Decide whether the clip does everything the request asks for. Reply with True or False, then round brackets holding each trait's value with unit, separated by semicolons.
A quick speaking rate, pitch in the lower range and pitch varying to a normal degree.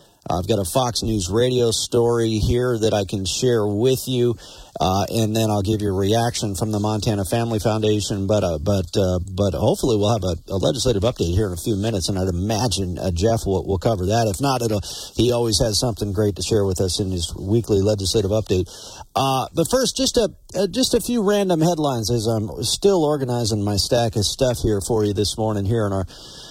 True (220 wpm; 110 Hz; 3.2 semitones)